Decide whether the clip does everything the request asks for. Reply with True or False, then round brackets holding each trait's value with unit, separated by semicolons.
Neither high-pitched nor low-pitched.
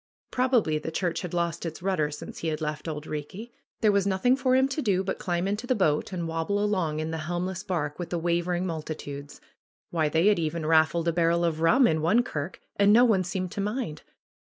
True (175 Hz)